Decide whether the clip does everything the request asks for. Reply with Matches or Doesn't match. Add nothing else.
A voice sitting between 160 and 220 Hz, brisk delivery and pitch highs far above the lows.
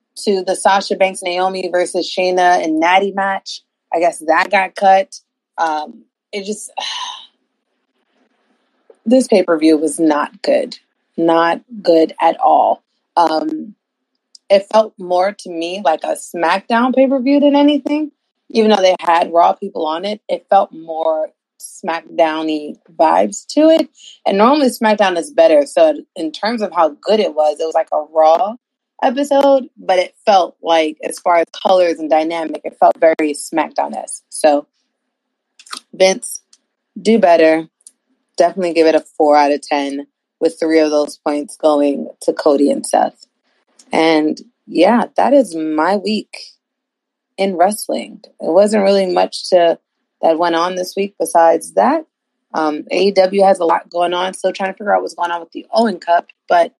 Doesn't match